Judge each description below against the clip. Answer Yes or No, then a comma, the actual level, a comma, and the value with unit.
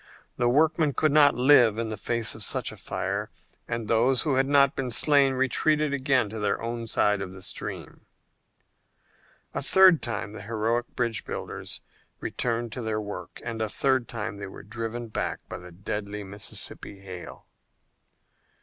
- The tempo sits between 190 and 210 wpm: No, average, 170 wpm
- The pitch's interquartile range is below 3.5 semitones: No, average, 3.8 semitones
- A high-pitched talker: No, low, 115 Hz